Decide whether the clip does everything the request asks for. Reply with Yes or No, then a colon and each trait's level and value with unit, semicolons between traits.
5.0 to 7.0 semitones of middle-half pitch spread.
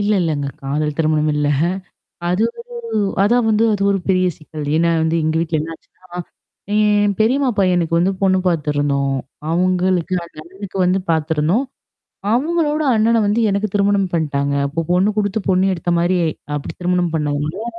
No: average, 4.5 semitones